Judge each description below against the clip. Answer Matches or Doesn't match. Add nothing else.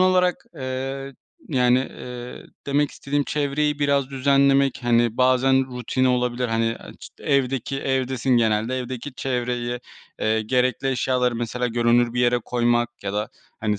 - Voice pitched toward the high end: Doesn't match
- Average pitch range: Doesn't match